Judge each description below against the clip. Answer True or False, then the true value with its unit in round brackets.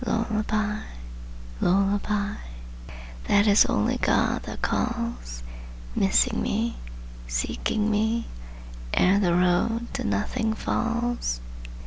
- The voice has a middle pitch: False (210 Hz)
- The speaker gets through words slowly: True (90 wpm)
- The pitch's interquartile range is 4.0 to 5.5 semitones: False (2.9 semitones)